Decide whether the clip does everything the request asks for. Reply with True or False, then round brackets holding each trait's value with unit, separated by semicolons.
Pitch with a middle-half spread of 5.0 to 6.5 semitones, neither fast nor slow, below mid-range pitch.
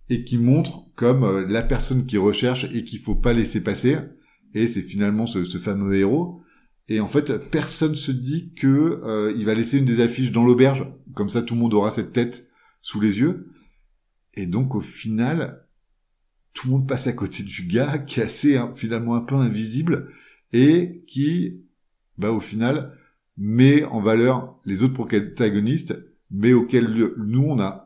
False (3.8 semitones; 180 wpm; 120 Hz)